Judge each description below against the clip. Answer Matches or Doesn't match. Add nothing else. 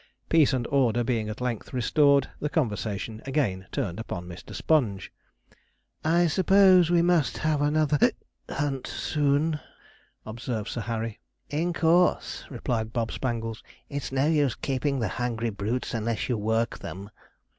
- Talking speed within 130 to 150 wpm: Matches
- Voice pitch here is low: Matches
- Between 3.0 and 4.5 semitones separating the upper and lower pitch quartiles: Doesn't match